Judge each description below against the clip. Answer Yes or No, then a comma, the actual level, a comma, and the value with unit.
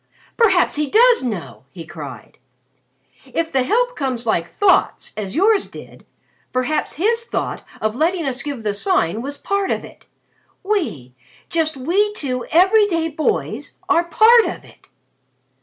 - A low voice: No, very high, 315 Hz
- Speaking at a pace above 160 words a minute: No, average, 150 wpm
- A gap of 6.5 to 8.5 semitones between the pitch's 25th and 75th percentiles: Yes, wide, 8.2 semitones